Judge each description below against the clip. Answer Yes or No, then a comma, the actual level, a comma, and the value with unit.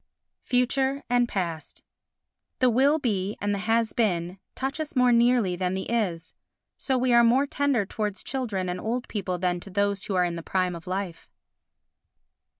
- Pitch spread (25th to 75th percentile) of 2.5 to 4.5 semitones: No, average, 5.2 semitones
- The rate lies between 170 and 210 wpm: Yes, average, 175 wpm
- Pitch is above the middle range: Yes, high, 210 Hz